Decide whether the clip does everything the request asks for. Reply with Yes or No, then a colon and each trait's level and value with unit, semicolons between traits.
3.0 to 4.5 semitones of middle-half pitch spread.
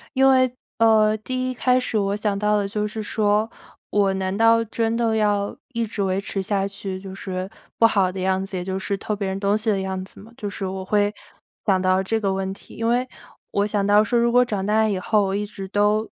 No: narrow, 2.4 semitones